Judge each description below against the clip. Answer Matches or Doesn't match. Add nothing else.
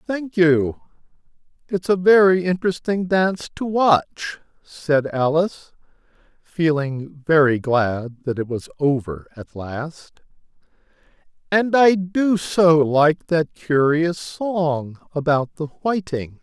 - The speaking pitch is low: Doesn't match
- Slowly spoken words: Matches